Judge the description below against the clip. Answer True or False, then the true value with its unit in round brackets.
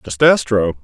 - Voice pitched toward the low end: True (105 Hz)